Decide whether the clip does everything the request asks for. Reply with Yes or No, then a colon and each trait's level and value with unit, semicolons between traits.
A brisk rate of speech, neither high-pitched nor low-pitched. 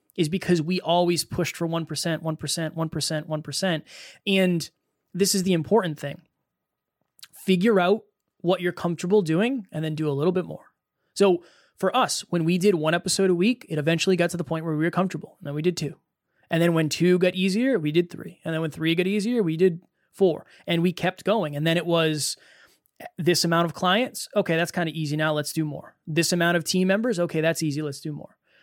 Yes: fast, 220 wpm; medium, 170 Hz